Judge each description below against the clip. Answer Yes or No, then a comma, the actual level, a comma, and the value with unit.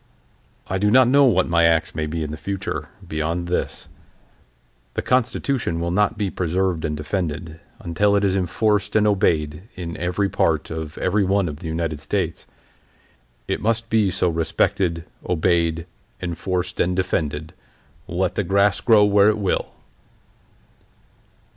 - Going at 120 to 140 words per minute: No, average, 150 wpm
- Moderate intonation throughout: Yes, average, 3.8 semitones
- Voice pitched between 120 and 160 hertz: No, very low, 90 Hz